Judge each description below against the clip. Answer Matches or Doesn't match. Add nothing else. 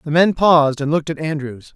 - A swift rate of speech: Matches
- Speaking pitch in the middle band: Matches